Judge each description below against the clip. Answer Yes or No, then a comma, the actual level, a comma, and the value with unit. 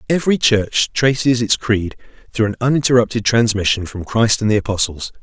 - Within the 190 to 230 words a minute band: No, average, 160 wpm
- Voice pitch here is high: No, low, 115 Hz